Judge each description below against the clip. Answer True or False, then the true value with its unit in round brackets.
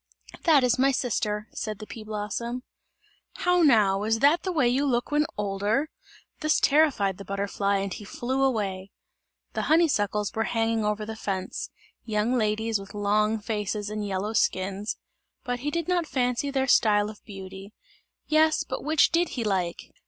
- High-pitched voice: True (220 Hz)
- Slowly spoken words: False (165 wpm)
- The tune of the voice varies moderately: True (4.6 semitones)